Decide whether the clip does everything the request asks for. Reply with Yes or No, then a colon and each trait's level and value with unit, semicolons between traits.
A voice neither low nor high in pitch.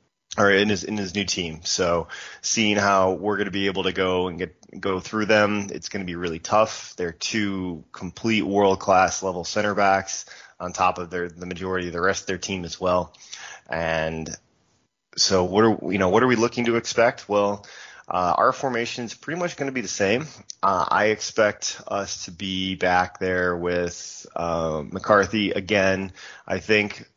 No: very low, 95 Hz